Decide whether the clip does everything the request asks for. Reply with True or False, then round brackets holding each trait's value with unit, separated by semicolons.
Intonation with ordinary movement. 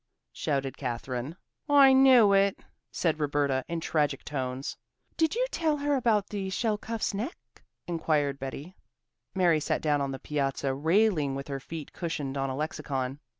False (7.1 semitones)